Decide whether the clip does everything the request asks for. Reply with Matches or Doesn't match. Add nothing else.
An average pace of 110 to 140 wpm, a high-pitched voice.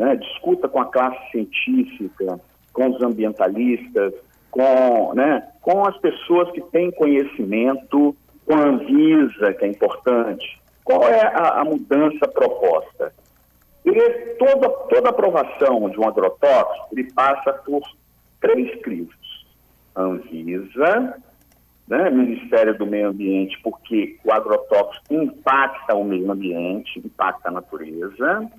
Doesn't match